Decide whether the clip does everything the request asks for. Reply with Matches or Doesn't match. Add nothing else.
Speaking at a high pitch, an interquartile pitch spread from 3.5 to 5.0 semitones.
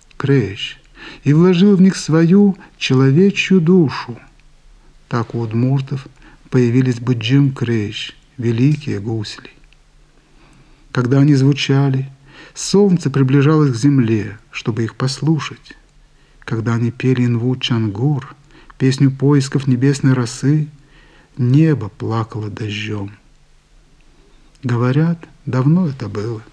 Doesn't match